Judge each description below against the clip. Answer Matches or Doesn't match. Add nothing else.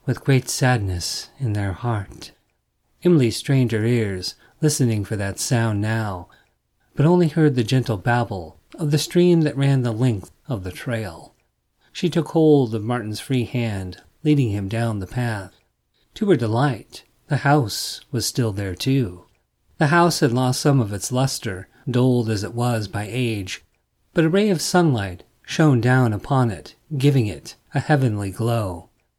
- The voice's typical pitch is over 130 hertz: Doesn't match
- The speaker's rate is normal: Matches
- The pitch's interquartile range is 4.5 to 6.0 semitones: Matches